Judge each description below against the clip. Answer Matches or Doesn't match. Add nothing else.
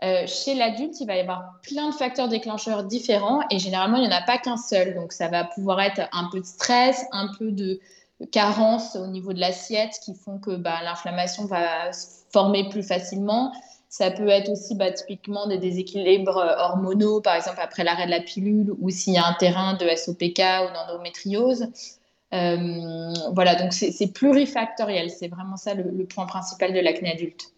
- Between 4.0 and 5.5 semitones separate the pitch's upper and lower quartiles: Doesn't match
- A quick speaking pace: Doesn't match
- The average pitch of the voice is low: Doesn't match